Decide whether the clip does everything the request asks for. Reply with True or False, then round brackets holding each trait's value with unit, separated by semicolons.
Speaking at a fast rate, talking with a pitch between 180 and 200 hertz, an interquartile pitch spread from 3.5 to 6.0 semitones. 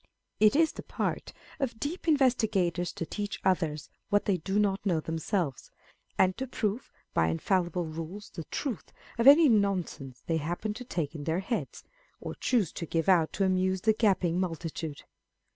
False (175 wpm; 185 Hz; 4.6 semitones)